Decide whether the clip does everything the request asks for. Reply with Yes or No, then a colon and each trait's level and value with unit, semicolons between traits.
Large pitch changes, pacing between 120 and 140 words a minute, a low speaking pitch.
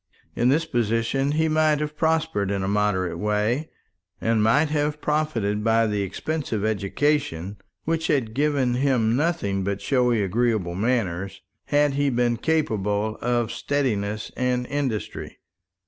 Yes: wide, 5.9 semitones; slow, 135 wpm; low, 120 Hz